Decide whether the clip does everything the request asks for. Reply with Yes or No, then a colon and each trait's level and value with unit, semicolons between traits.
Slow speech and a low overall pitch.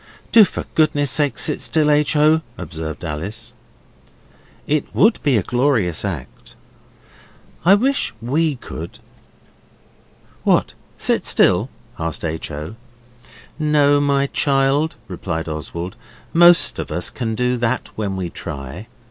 Yes: slow, 125 wpm; low, 125 Hz